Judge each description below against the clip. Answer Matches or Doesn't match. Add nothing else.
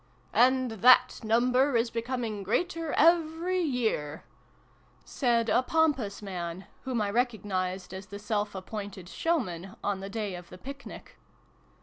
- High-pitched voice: Matches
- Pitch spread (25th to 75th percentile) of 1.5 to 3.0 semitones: Doesn't match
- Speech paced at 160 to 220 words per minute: Doesn't match